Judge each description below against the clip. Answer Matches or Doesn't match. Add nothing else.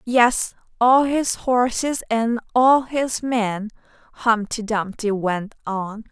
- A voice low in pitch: Doesn't match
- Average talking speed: Doesn't match